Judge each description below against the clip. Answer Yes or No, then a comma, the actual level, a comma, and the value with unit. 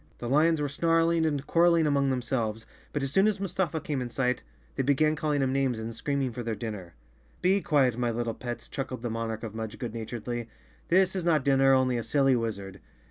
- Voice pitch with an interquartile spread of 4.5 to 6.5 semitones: Yes, average, 4.9 semitones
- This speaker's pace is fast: Yes, fast, 215 wpm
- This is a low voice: Yes, low, 130 Hz